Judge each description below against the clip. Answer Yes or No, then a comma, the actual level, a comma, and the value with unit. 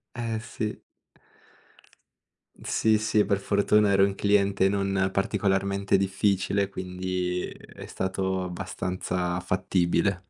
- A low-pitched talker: Yes, very low, 95 Hz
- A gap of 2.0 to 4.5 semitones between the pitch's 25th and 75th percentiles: No, narrow, 1.4 semitones